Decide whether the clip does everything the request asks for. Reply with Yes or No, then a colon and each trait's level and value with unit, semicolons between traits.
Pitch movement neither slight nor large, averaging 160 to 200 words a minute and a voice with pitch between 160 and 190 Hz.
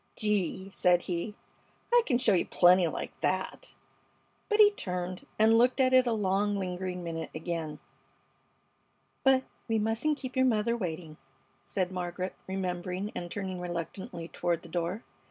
No: average, 4.1 semitones; average, 150 wpm; medium, 185 Hz